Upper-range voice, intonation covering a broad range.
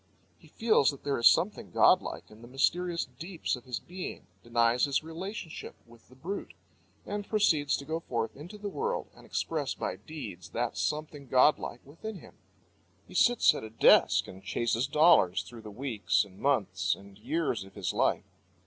No: medium, 140 Hz; wide, 6.5 semitones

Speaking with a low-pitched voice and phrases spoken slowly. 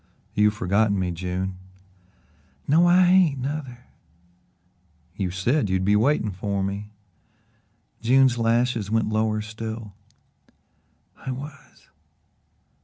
Yes: low, 110 Hz; slow, 105 wpm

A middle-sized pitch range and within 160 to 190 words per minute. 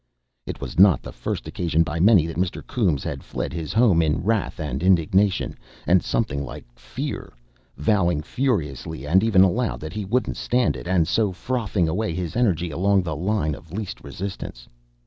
Yes: average, 4.6 semitones; average, 180 wpm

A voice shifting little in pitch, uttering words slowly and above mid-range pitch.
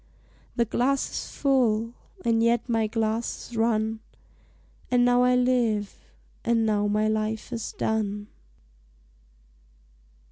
Yes: narrow, 2.0 semitones; slow, 115 wpm; high, 225 Hz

